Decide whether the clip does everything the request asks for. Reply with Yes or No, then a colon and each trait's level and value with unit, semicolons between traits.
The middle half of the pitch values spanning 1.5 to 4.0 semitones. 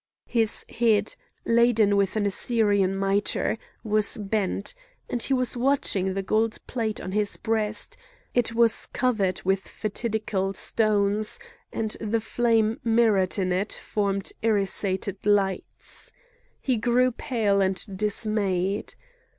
Yes: narrow, 2.5 semitones